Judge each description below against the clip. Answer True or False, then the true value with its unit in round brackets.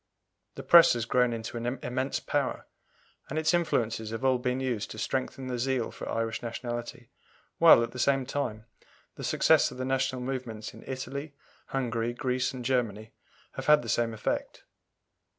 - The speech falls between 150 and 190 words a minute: True (170 wpm)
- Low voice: True (125 Hz)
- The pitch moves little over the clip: True (2.3 semitones)